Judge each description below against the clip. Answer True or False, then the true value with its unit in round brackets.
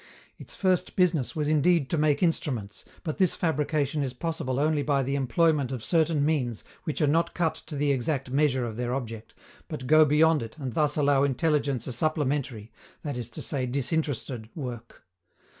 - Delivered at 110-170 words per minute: False (180 wpm)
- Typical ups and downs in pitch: True (3.5 semitones)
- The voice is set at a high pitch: False (145 Hz)